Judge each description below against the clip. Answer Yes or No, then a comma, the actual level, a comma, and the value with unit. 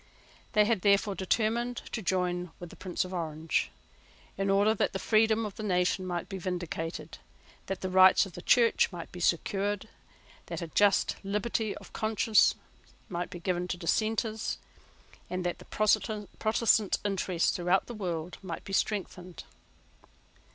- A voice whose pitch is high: Yes, high, 195 Hz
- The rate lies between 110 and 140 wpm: No, average, 155 wpm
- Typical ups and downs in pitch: Yes, average, 3.2 semitones